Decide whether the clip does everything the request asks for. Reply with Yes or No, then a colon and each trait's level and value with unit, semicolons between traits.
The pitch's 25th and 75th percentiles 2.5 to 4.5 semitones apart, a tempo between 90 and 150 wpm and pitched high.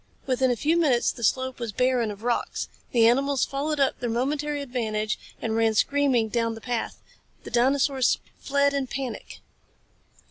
No: average, 3.3 semitones; average, 165 wpm; very high, 255 Hz